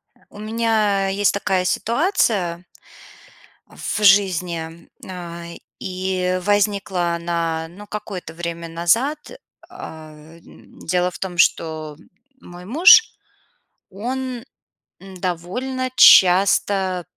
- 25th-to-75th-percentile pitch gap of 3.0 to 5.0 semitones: Yes, average, 3.4 semitones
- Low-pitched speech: No, medium, 185 Hz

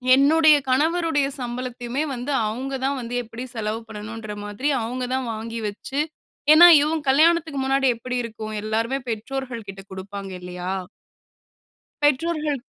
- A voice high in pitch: Yes, very high, 250 Hz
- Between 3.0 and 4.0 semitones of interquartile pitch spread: No, average, 4.5 semitones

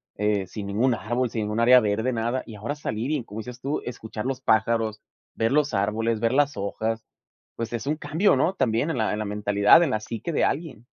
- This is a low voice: Yes, low, 115 Hz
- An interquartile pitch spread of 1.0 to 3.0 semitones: No, average, 3.4 semitones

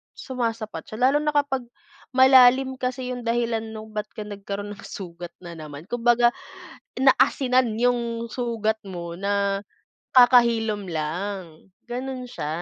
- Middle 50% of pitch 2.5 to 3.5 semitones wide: No, average, 4.0 semitones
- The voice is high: Yes, high, 230 Hz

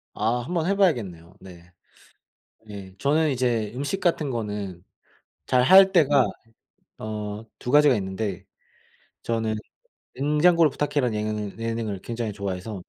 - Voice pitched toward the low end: Yes, low, 115 Hz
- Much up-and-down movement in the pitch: Yes, wide, 6.1 semitones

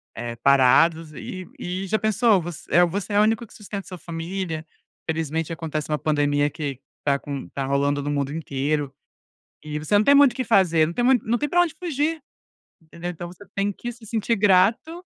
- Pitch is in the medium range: Yes, medium, 170 Hz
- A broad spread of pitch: Yes, wide, 6.1 semitones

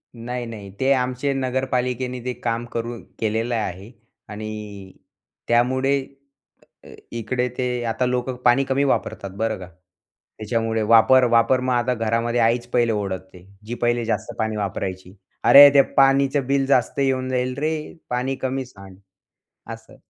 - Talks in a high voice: No, low, 120 Hz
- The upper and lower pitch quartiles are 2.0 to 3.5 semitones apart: Yes, average, 2.8 semitones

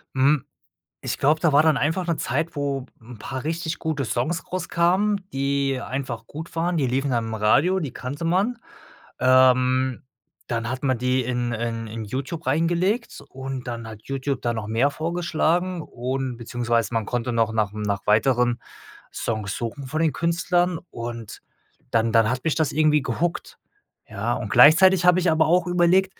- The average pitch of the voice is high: No, low, 135 Hz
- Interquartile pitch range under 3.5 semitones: No, wide, 5.6 semitones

